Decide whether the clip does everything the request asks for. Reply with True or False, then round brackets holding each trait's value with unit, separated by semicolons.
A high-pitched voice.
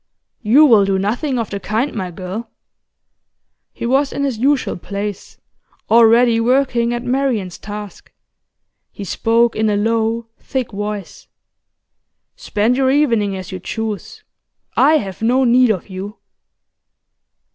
True (225 Hz)